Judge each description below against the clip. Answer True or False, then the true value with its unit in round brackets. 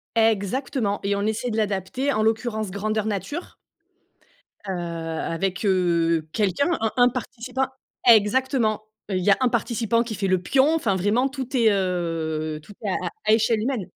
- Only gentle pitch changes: False (4.3 semitones)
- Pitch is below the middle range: False (215 Hz)